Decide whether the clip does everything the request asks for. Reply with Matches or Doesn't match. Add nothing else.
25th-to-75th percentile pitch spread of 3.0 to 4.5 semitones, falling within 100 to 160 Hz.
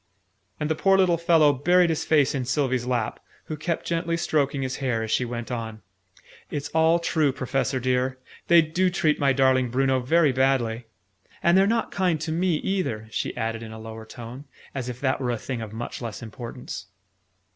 Doesn't match